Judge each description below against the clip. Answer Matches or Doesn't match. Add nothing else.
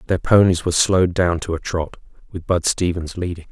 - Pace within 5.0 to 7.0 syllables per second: Matches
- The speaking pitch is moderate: Doesn't match